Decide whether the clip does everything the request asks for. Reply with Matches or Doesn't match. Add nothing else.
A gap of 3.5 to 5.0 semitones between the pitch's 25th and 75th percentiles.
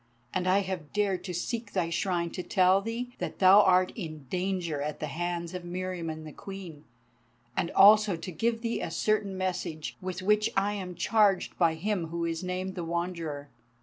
Doesn't match